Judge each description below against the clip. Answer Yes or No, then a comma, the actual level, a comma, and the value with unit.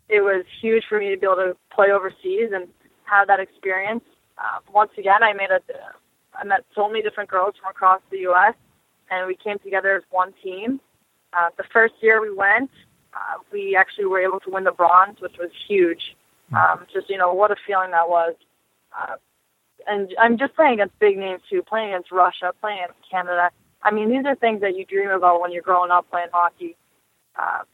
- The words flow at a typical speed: No, fast, 210 wpm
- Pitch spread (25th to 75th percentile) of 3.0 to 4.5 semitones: No, narrow, 2.6 semitones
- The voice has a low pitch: No, high, 195 Hz